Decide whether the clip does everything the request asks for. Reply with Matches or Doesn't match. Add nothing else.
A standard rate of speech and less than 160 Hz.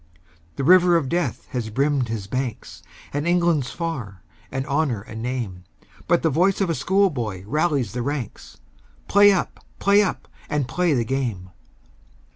Matches